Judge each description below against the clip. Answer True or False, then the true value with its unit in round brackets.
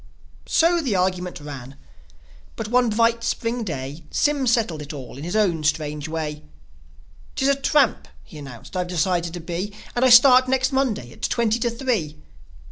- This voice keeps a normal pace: True (170 wpm)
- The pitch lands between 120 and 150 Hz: False (195 Hz)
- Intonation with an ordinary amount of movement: False (8.0 semitones)